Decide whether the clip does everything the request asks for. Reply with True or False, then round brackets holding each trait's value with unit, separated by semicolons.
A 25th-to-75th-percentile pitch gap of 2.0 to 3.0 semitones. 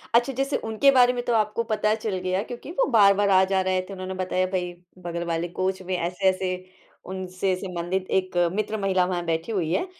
True (2.7 semitones)